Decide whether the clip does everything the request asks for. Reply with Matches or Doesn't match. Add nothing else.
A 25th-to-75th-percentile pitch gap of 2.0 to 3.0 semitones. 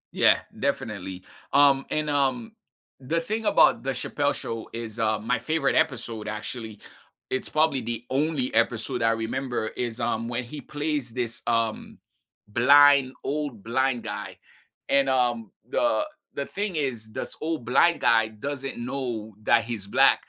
Doesn't match